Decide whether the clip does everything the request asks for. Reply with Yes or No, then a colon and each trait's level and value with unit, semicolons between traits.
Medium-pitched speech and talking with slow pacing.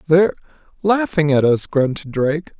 Yes: medium, 155 Hz; slow, 115 wpm